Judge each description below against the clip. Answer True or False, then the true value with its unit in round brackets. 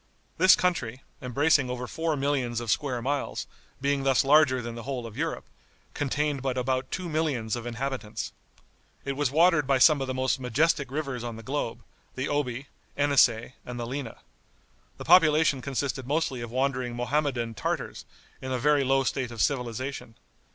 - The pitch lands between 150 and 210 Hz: False (130 Hz)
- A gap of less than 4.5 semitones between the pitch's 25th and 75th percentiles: True (2.9 semitones)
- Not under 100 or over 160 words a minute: False (170 wpm)